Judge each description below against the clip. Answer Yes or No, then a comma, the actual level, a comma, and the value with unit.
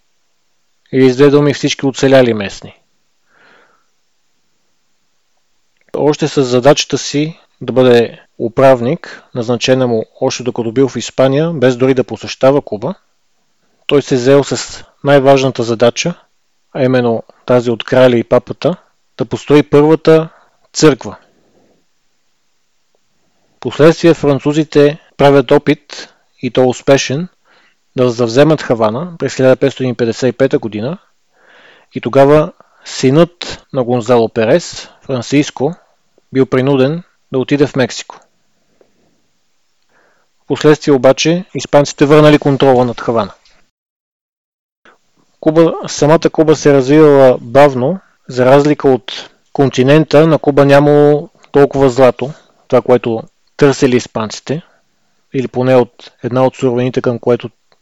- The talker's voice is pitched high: No, low, 135 Hz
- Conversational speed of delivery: No, slow, 105 wpm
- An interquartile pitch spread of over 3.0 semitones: No, narrow, 2.6 semitones